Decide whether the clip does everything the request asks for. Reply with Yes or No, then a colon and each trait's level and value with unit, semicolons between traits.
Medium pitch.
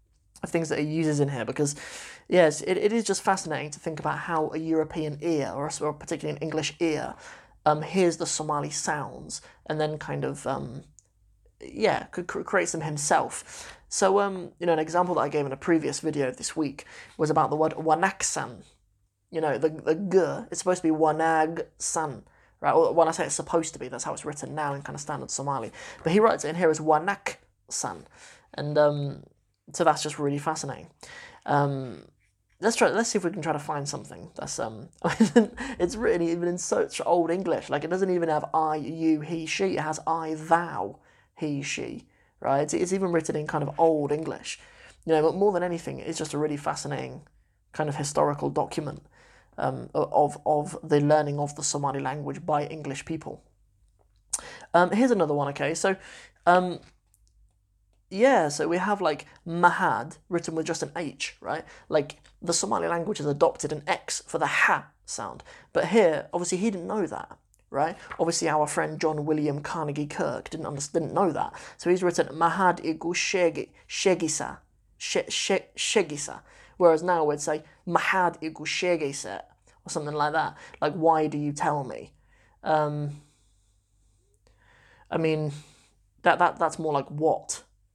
Yes: medium, 155 Hz